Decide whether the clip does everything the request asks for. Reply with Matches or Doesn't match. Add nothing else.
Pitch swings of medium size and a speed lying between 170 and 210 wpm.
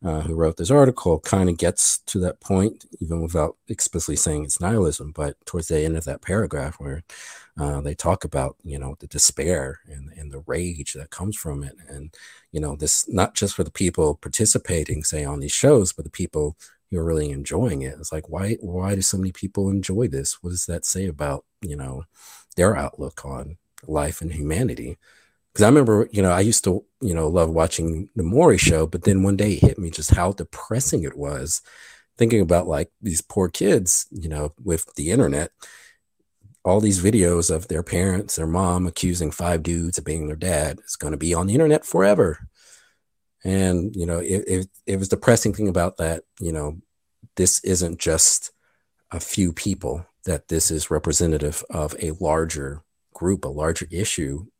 Matches